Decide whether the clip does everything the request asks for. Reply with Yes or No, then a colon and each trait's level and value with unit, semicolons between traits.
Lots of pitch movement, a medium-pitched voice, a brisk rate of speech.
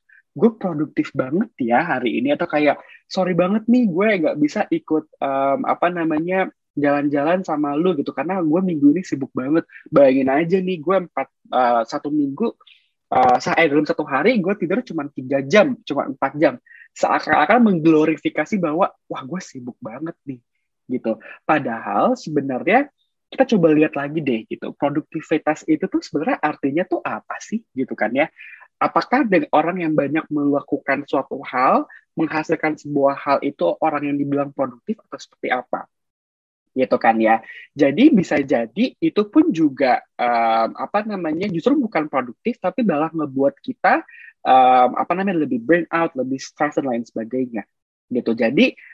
Yes: wide, 6.4 semitones; medium, 160 Hz; fast, 155 wpm